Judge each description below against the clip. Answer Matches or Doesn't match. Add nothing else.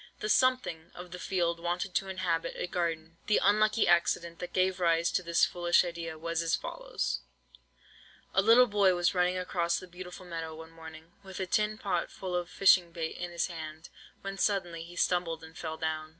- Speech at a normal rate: Matches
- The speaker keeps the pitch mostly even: Matches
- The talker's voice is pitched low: Doesn't match